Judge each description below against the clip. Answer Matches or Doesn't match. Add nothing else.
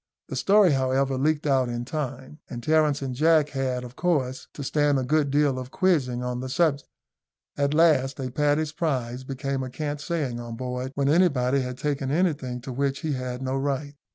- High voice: Doesn't match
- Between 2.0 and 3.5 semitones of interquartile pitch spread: Matches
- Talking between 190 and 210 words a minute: Matches